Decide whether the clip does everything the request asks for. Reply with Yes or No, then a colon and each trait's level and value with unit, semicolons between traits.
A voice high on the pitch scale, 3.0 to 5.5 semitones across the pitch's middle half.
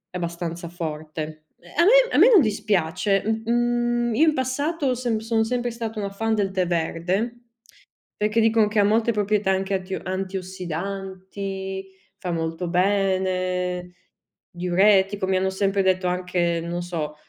Yes: high, 195 Hz; average, 3.6 semitones